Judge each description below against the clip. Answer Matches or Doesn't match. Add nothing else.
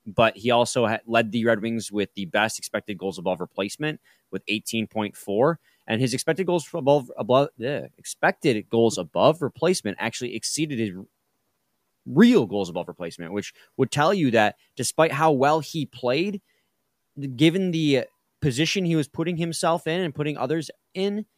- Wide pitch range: Matches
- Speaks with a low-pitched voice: Matches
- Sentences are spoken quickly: Doesn't match